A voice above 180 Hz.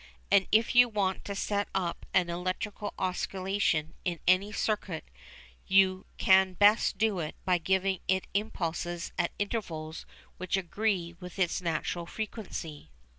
Yes: high, 190 Hz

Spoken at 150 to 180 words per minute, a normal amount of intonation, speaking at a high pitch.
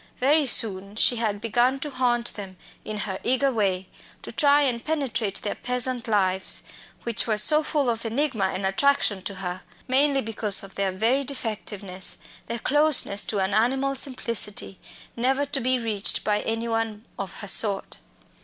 Yes: average, 165 wpm; average, 4.6 semitones; high, 230 Hz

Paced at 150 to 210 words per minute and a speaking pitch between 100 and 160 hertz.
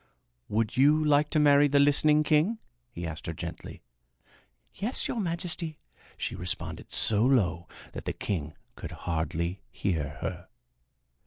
No: average, 140 wpm; medium, 140 Hz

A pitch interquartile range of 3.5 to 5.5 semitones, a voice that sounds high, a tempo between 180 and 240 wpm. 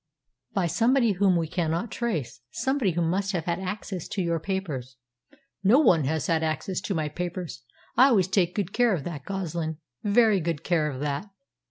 No: average, 3.9 semitones; medium, 175 Hz; average, 185 wpm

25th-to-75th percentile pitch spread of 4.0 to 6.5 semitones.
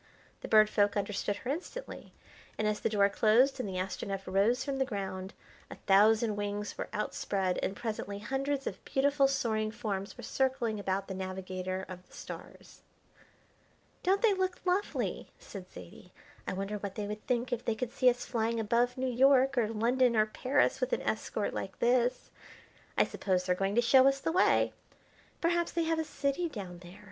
Yes: average, 5.1 semitones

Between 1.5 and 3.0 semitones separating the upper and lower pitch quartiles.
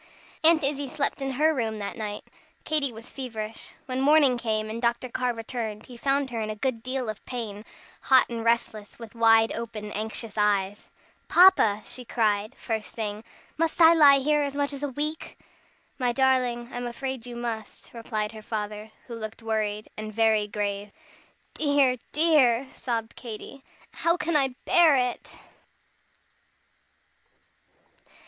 No: average, 3.9 semitones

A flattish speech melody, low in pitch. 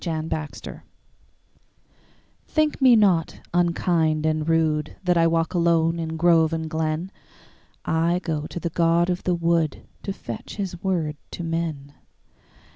No: narrow, 1.7 semitones; medium, 165 Hz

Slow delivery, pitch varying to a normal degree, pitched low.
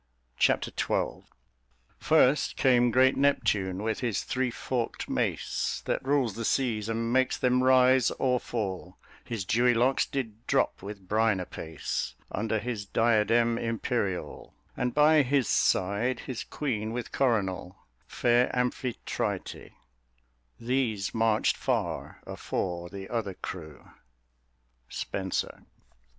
Yes: slow, 115 wpm; average, 3.7 semitones; low, 115 Hz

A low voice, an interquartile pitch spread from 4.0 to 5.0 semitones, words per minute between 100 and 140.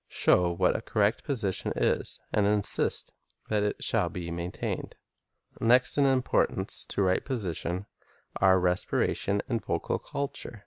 Yes: low, 100 Hz; average, 4.4 semitones; slow, 135 wpm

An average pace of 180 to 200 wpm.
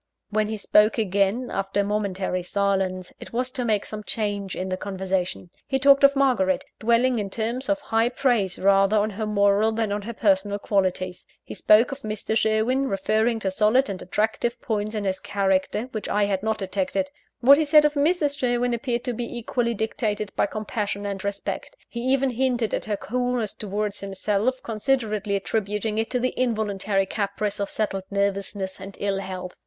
Yes: average, 185 wpm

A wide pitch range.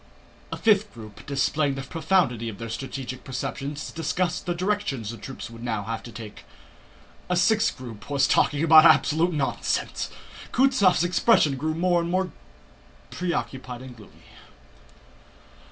Yes: wide, 6.5 semitones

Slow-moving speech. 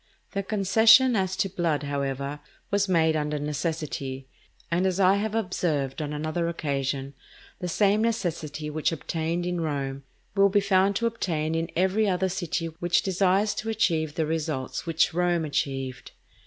No: average, 155 wpm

